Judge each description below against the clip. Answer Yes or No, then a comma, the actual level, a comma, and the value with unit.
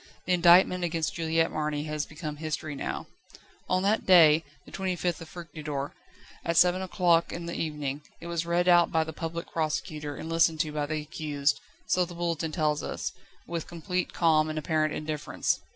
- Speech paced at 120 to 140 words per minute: No, average, 175 wpm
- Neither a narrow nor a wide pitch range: No, narrow, 2.1 semitones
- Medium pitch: Yes, medium, 160 Hz